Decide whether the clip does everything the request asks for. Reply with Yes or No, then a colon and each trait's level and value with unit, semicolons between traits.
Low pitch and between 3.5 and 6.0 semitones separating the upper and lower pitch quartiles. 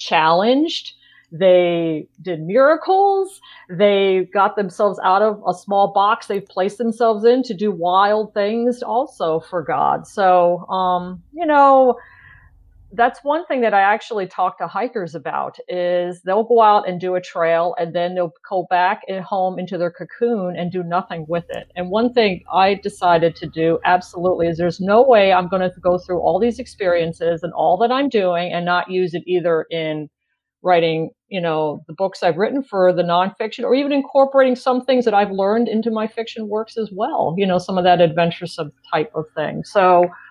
No: medium, 185 Hz; average, 4.2 semitones